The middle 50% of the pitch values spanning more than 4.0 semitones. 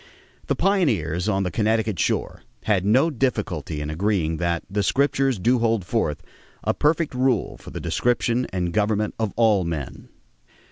Yes: wide, 5.6 semitones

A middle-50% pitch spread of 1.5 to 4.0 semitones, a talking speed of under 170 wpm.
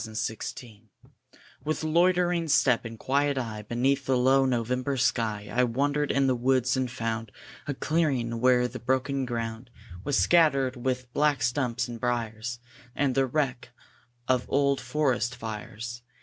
Yes: average, 2.7 semitones; average, 150 wpm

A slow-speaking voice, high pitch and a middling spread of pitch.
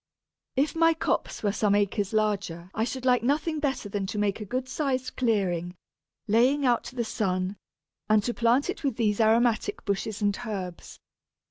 No: average, 175 wpm; high, 220 Hz; average, 4.1 semitones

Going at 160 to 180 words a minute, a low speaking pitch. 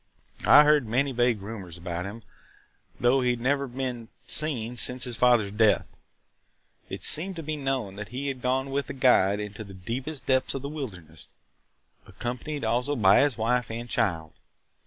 Yes: average, 175 wpm; low, 120 Hz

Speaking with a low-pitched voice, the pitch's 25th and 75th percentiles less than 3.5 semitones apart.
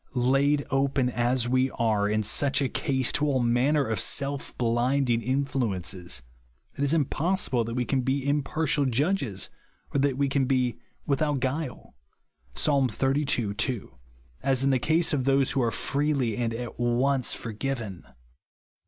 Yes: low, 130 Hz; average, 2.8 semitones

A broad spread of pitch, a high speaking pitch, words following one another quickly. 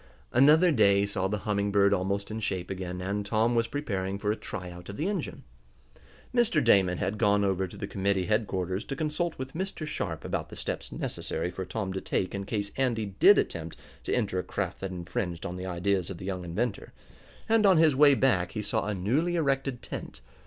No: wide, 5.7 semitones; low, 100 Hz; fast, 210 wpm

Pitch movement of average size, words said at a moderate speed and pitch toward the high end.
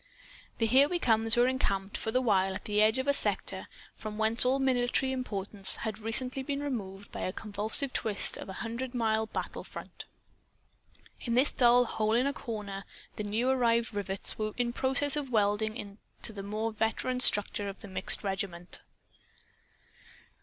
Yes: average, 3.6 semitones; average, 175 wpm; high, 225 Hz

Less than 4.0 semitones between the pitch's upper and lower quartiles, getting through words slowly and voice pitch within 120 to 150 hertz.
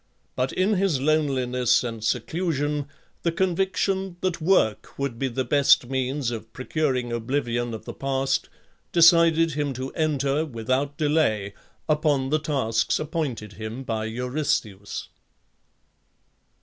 No: average, 4.4 semitones; slow, 125 wpm; low, 135 Hz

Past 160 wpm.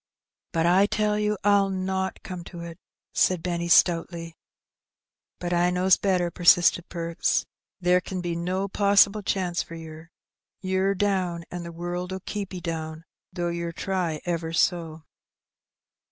No: average, 150 wpm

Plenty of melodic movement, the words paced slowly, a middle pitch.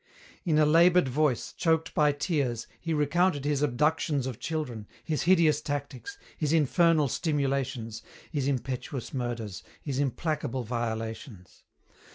No: average, 4.1 semitones; slow, 125 wpm; medium, 145 Hz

